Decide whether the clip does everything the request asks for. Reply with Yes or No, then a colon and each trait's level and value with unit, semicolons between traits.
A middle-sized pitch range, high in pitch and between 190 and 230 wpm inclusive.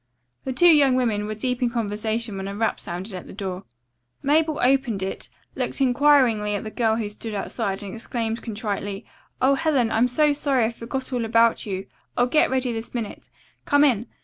Yes: average, 4.0 semitones; high, 230 Hz; average, 195 wpm